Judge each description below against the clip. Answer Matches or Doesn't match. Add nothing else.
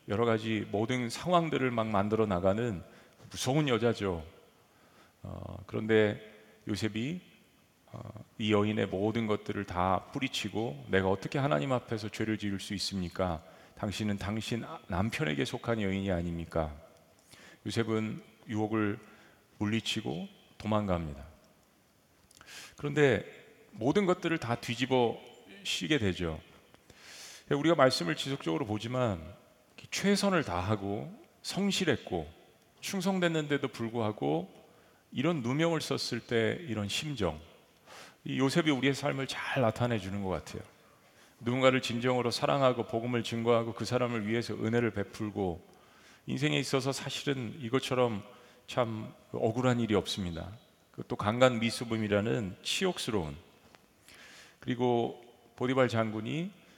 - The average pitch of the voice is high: Doesn't match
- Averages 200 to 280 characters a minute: Matches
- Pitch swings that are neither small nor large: Matches